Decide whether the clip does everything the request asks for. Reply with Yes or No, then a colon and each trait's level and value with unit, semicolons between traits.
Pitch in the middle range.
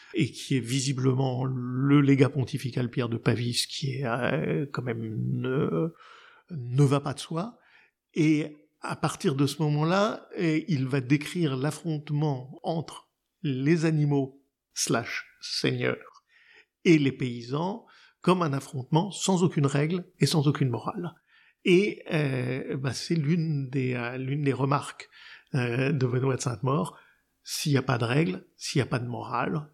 Yes: medium, 145 Hz